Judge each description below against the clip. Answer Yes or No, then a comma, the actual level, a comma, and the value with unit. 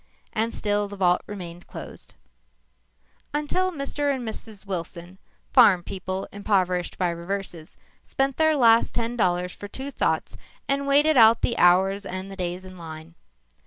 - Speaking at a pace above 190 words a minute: No, average, 150 wpm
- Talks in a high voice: Yes, high, 200 Hz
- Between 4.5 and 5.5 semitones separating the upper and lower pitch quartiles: Yes, average, 4.9 semitones